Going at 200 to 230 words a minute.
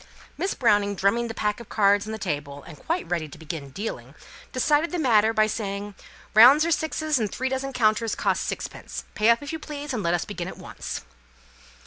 Yes: fast, 205 wpm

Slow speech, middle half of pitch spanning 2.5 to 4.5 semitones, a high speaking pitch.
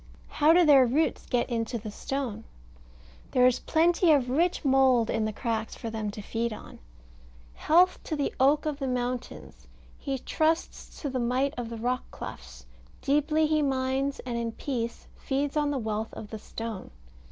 No: average, 175 wpm; average, 4.1 semitones; very high, 255 Hz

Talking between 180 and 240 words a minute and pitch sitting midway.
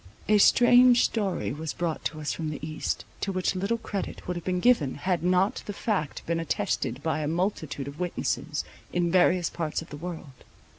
Yes: average, 195 wpm; medium, 175 Hz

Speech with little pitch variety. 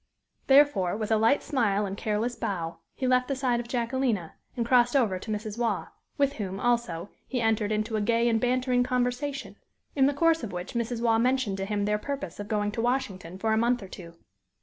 No: average, 3.4 semitones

